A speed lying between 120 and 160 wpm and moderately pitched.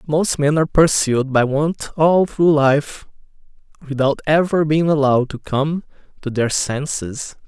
Yes: average, 145 wpm; medium, 145 Hz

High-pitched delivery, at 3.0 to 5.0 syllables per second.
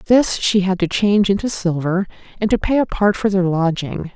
No: high, 195 Hz; 5.2 syllables/s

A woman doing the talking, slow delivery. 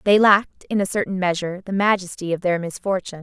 No: female; fast, 205 wpm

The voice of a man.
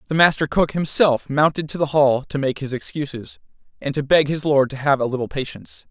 Yes: male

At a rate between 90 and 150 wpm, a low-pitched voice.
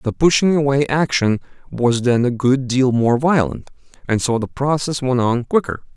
No: average, 180 wpm; low, 130 Hz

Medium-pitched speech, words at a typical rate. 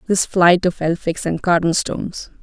Yes: medium, 175 Hz; average, 150 wpm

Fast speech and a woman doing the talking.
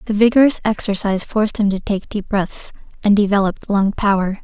No: average, 175 wpm; female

